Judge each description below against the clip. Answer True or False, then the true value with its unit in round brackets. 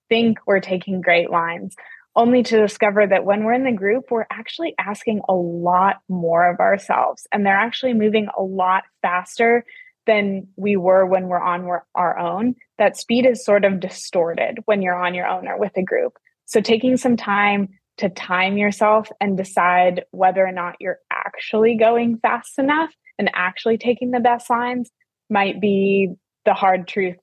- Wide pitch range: False (3.9 semitones)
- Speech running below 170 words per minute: False (175 wpm)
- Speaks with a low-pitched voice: False (205 Hz)